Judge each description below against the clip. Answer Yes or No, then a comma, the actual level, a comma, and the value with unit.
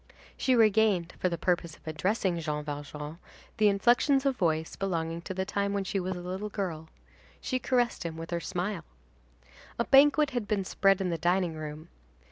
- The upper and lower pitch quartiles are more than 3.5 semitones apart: Yes, average, 4.4 semitones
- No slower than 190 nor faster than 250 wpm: No, average, 180 wpm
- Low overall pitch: No, medium, 185 Hz